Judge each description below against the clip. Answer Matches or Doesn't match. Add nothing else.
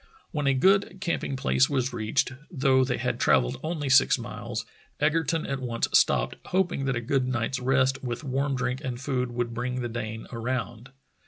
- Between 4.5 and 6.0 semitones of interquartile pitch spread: Doesn't match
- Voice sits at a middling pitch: Doesn't match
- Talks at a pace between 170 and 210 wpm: Matches